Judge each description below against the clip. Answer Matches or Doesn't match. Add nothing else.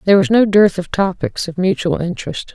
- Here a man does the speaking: Doesn't match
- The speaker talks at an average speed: Doesn't match